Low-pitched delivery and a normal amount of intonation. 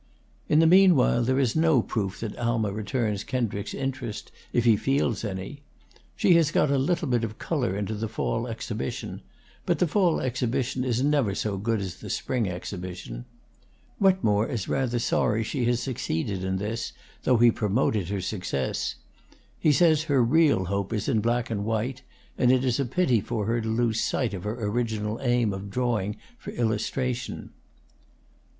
Yes: low, 115 Hz; average, 3.9 semitones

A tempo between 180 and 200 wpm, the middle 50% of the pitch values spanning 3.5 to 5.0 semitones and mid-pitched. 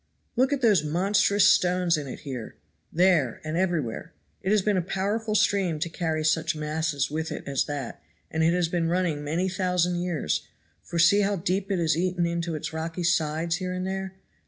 No: average, 195 wpm; average, 3.1 semitones; medium, 175 Hz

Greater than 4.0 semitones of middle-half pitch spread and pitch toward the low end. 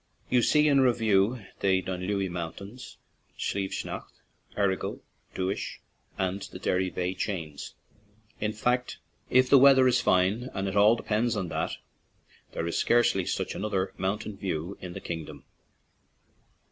Yes: average, 4.4 semitones; low, 100 Hz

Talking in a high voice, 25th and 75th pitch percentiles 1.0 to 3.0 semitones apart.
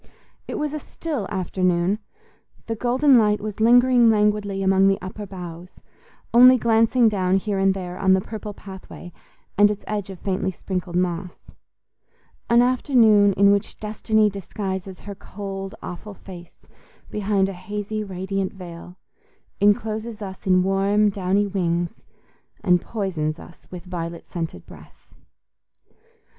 Yes: high, 195 Hz; narrow, 2.5 semitones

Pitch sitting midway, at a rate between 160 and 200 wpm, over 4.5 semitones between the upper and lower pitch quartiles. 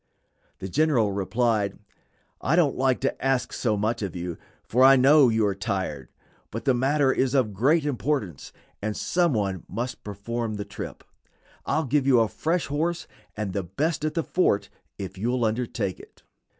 No: low, 120 Hz; average, 175 wpm; wide, 5.4 semitones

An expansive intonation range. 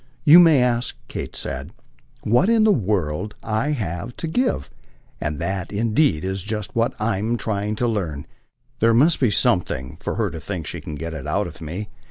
Yes: wide, 5.8 semitones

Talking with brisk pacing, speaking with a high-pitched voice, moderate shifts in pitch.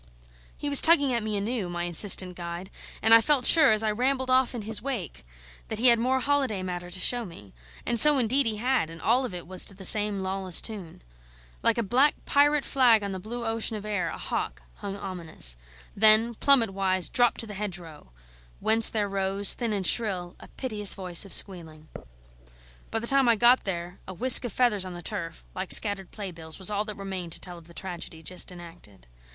Yes: fast, 215 wpm; high, 205 Hz; average, 4.7 semitones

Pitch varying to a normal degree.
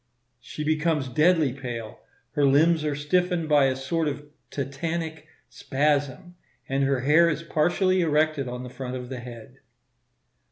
Yes: average, 3.3 semitones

